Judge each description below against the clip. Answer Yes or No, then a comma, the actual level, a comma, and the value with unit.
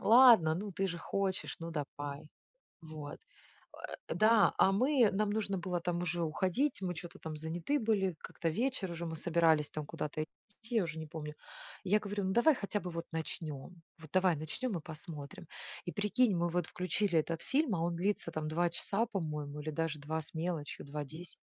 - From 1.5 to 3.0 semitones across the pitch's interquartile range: No, average, 4.1 semitones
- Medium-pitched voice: Yes, medium, 175 Hz